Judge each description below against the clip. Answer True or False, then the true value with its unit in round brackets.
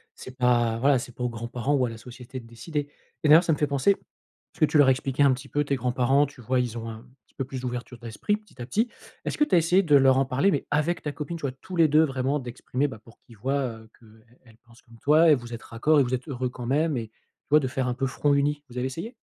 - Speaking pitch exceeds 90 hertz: True (130 Hz)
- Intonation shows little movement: False (3.3 semitones)